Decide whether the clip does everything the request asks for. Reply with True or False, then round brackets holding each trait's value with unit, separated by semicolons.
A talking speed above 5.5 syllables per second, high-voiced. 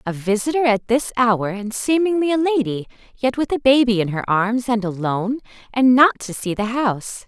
False (5.1 syllables/s; 235 Hz)